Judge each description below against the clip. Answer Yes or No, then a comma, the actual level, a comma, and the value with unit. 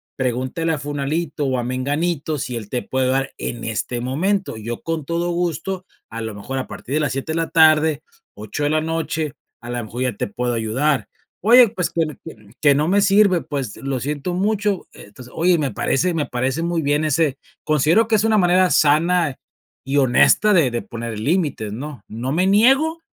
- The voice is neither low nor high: Yes, medium, 150 Hz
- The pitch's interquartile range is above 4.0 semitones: Yes, average, 5.2 semitones